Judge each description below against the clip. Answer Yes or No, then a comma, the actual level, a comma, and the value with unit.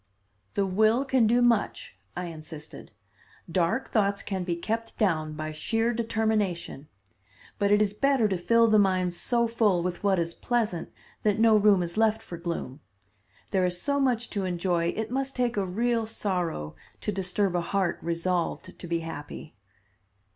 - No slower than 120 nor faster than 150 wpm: No, average, 170 wpm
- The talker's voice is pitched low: No, high, 195 Hz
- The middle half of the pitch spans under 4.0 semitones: No, average, 4.5 semitones